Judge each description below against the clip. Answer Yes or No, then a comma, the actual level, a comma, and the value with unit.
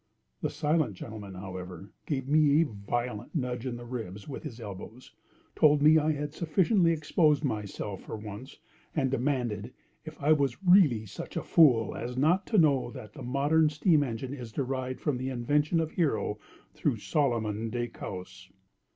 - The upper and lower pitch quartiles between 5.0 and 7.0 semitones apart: Yes, average, 5.3 semitones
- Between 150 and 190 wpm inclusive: Yes, average, 160 wpm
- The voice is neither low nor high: No, low, 130 Hz